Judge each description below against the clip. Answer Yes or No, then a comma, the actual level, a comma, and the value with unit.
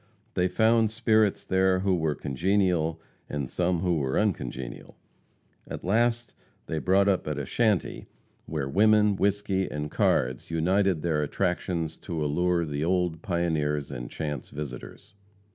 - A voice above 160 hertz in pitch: No, very low, 90 Hz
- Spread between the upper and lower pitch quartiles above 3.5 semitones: Yes, average, 4.7 semitones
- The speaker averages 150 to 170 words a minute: No, average, 140 wpm